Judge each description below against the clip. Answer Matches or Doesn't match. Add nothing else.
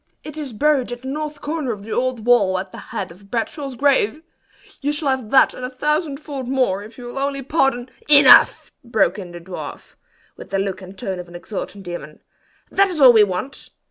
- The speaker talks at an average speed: Doesn't match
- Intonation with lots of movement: Matches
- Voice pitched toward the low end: Doesn't match